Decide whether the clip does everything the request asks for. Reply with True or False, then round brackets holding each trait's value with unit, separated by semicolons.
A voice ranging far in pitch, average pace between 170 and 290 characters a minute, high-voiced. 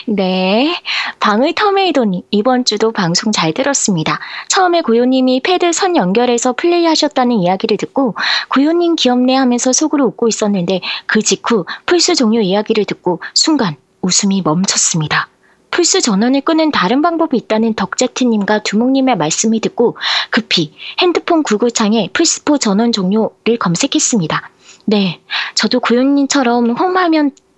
False (5.9 semitones; 325 characters per minute; 240 Hz)